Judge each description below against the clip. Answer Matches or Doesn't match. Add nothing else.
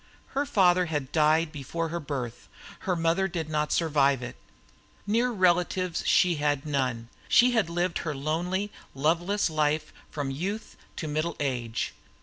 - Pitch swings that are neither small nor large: Matches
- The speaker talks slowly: Doesn't match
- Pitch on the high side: Doesn't match